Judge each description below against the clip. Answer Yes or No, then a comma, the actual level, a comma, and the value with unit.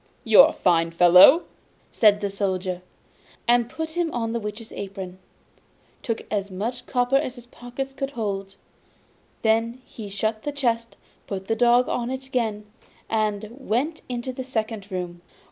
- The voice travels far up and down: No, average, 3.8 semitones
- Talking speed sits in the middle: Yes, average, 160 wpm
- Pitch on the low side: No, high, 225 Hz